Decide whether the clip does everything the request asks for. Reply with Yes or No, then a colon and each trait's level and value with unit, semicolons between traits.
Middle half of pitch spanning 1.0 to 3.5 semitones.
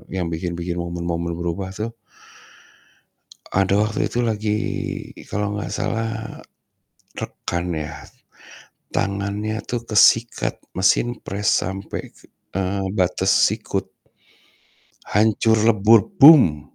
No: average, 3.9 semitones